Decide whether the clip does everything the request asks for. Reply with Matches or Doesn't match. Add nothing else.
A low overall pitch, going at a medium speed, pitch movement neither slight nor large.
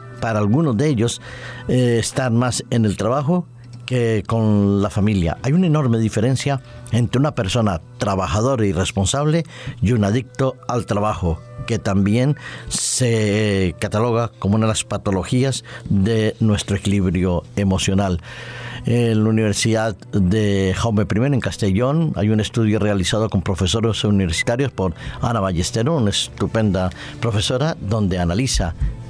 Matches